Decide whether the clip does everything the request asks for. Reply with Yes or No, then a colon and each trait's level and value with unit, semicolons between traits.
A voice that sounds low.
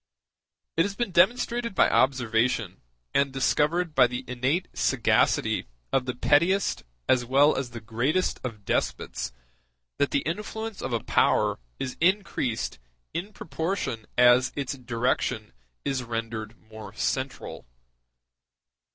Yes: low, 130 Hz